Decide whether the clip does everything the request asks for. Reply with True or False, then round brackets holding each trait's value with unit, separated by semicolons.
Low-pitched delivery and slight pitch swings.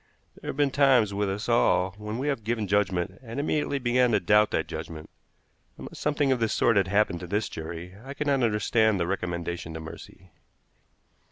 False (105 Hz; 5.4 semitones)